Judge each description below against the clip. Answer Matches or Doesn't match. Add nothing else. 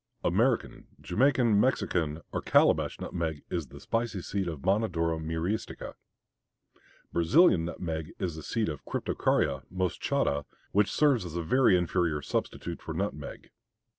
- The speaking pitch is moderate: Doesn't match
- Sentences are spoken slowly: Matches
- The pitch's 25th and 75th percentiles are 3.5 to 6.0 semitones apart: Matches